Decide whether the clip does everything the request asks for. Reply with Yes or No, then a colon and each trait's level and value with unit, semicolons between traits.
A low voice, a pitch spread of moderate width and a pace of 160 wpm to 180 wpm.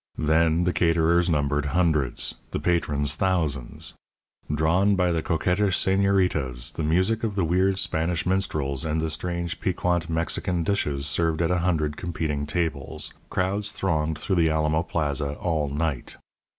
No: very low, 80 Hz; average, 3.0 semitones; average, 140 wpm